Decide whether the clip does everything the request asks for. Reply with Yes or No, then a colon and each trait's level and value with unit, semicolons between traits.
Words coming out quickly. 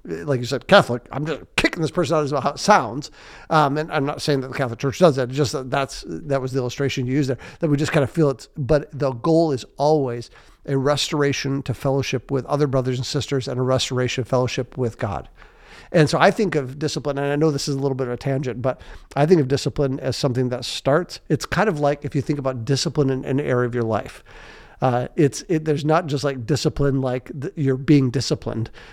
Yes: fast, 245 wpm